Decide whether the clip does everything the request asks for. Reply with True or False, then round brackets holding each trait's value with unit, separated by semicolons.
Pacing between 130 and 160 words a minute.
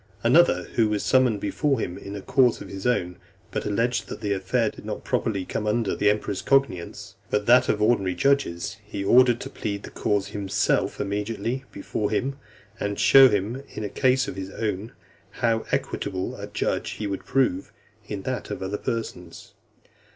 False (185 wpm)